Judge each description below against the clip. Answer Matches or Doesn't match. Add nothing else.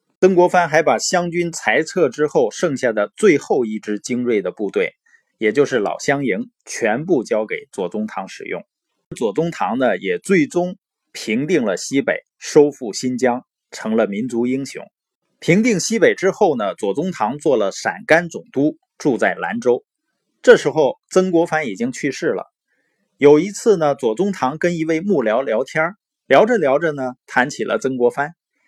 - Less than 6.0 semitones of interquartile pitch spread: Doesn't match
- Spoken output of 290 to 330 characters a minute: Doesn't match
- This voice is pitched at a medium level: Matches